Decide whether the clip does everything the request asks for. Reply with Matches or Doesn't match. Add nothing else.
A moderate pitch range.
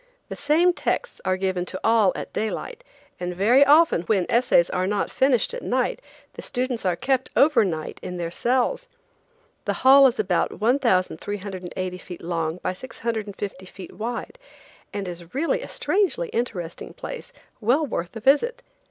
Doesn't match